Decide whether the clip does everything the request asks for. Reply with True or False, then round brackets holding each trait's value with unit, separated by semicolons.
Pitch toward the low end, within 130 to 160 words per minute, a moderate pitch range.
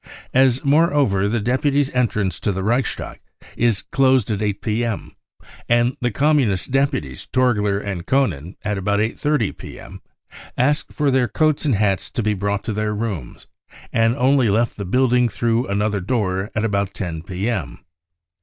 True (110 Hz; 155 wpm; 4.3 semitones)